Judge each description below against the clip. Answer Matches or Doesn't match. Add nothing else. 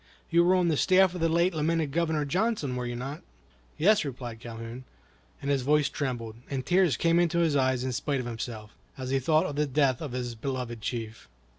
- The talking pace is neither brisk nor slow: Doesn't match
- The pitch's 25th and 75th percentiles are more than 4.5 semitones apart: Matches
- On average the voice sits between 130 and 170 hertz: Matches